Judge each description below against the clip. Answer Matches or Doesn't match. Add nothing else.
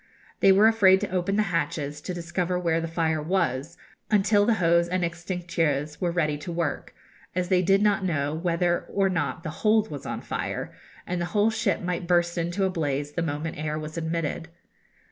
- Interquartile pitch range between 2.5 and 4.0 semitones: Matches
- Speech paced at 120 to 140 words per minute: Doesn't match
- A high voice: Doesn't match